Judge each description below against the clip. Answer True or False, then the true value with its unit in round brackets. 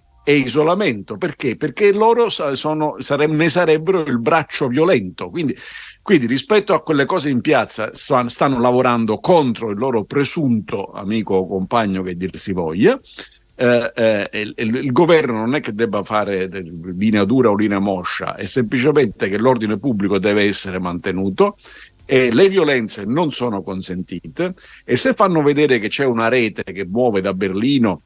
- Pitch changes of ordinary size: False (6.9 semitones)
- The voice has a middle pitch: False (120 Hz)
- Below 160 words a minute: False (165 wpm)